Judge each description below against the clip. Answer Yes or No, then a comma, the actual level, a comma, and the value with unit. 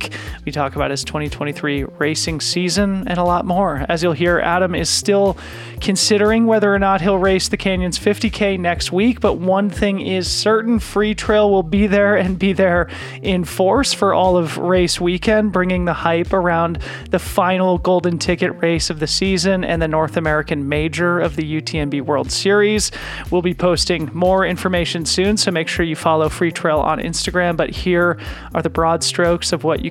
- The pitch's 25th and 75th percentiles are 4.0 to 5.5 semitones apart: No, average, 2.9 semitones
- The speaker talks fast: No, average, 190 wpm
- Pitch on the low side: No, medium, 180 Hz